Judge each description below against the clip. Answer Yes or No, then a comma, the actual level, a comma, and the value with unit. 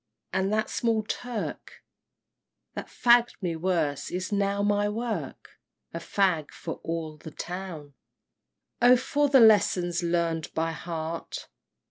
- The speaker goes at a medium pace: No, slow, 130 wpm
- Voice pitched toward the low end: No, medium, 185 Hz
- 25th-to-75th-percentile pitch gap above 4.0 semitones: Yes, average, 4.7 semitones